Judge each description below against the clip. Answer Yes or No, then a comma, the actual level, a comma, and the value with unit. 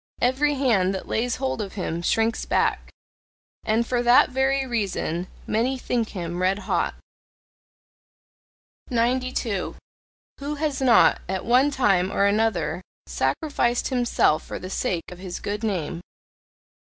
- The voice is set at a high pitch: Yes, high, 225 Hz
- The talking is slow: Yes, slow, 130 wpm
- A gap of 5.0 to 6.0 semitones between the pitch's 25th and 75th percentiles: Yes, average, 5.3 semitones